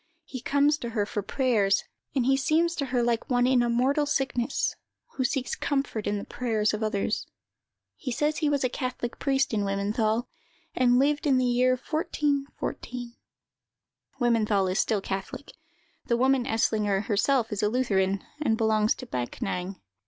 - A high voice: Yes, high, 245 Hz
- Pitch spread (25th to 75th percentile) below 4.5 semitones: Yes, average, 4.0 semitones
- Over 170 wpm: No, average, 165 wpm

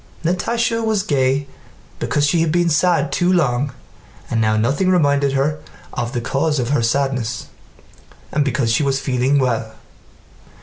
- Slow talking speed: No, average, 150 wpm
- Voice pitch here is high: No, medium, 140 Hz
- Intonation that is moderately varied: Yes, average, 4.6 semitones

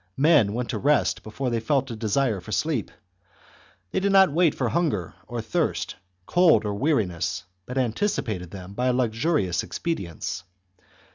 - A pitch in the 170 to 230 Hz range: No, low, 125 Hz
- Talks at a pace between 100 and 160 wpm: Yes, average, 155 wpm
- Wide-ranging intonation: Yes, wide, 6.9 semitones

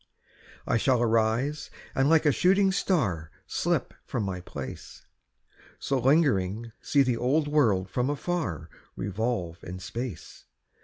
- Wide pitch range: Yes, wide, 7.2 semitones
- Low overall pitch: Yes, low, 120 Hz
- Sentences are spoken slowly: Yes, slow, 125 wpm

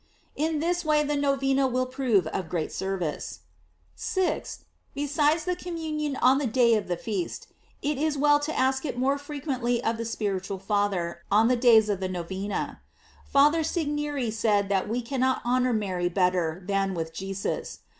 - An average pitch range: No, wide, 6.8 semitones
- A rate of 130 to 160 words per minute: No, average, 170 wpm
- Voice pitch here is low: No, high, 245 Hz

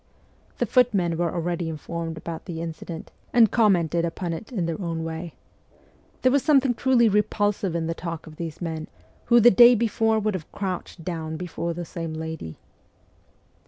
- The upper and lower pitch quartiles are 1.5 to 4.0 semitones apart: No, average, 4.5 semitones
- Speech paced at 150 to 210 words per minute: Yes, average, 170 wpm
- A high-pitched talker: No, medium, 170 Hz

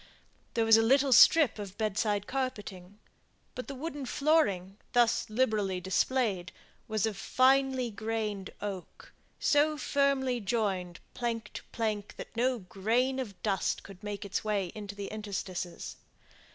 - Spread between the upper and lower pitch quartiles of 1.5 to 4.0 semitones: No, average, 4.4 semitones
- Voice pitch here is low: No, high, 220 Hz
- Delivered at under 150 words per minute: Yes, average, 140 wpm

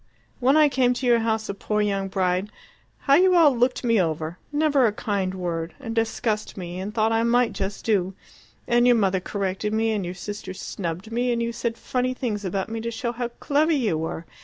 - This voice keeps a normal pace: No, fast, 215 wpm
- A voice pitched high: Yes, high, 220 Hz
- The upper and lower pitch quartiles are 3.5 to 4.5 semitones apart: Yes, average, 4.2 semitones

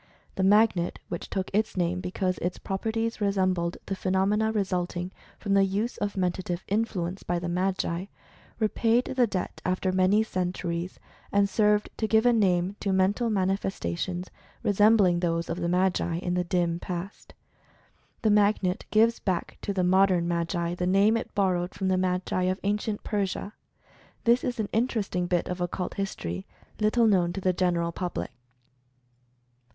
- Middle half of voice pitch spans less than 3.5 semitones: Yes, narrow, 2.6 semitones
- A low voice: No, high, 190 Hz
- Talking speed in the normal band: Yes, average, 155 wpm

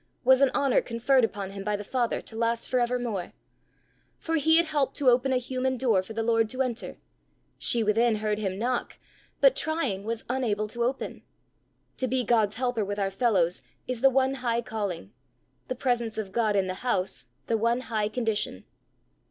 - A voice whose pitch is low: No, high, 235 Hz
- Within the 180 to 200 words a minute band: Yes, average, 190 wpm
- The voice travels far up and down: No, average, 3.4 semitones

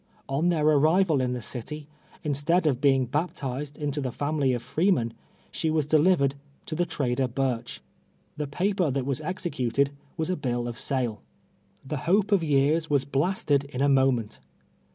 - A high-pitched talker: No, medium, 145 Hz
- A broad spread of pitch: No, average, 3.3 semitones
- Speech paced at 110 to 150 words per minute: No, average, 170 wpm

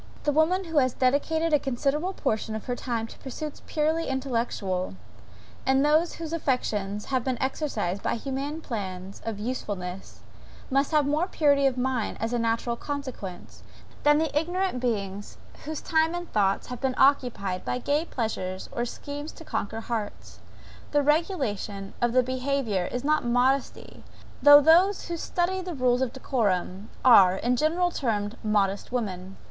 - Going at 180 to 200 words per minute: No, average, 155 wpm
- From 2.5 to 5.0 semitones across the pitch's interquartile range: No, wide, 5.5 semitones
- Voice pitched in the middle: No, very high, 255 Hz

